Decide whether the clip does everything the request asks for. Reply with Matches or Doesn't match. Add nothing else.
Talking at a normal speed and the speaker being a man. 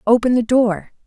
Doesn't match